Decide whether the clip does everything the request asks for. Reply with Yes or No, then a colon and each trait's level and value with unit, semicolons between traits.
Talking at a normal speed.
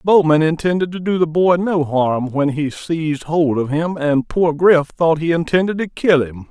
No: fast, 210 wpm